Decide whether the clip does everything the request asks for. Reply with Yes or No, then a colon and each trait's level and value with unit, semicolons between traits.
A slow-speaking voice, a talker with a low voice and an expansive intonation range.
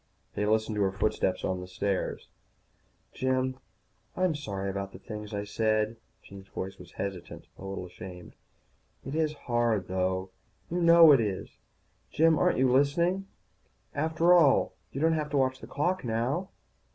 No: average, 160 wpm; low, 115 Hz; wide, 7.6 semitones